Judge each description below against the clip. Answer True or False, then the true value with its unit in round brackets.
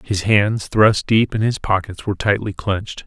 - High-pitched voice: False (100 Hz)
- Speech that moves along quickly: False (195 wpm)